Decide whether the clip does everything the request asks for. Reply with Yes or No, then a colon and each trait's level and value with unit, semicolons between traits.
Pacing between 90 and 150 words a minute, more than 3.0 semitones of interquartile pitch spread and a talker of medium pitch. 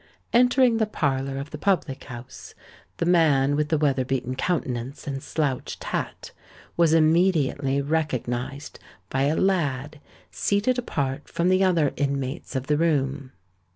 Yes: average, 140 wpm; average, 4.0 semitones; medium, 145 Hz